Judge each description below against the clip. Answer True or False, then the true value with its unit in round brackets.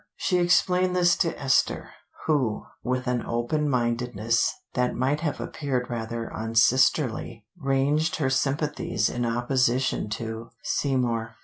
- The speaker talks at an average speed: False (120 wpm)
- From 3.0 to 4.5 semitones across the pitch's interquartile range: True (3.9 semitones)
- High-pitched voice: False (125 Hz)